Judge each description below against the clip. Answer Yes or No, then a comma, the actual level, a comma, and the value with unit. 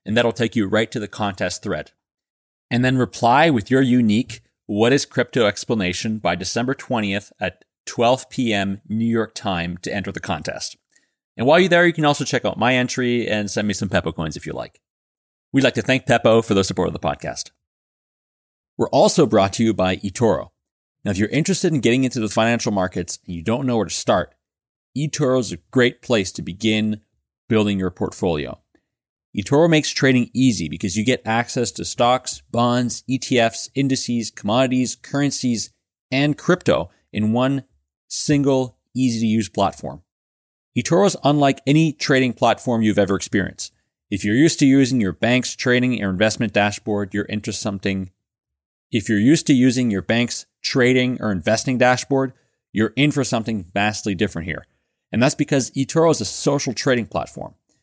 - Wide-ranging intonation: No, average, 4.0 semitones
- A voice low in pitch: Yes, low, 115 Hz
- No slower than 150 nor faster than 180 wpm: Yes, average, 175 wpm